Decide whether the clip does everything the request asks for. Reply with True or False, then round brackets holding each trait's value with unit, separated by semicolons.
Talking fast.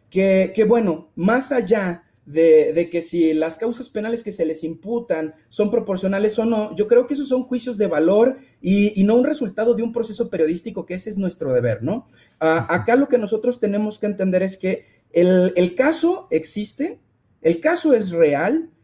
True (195 wpm)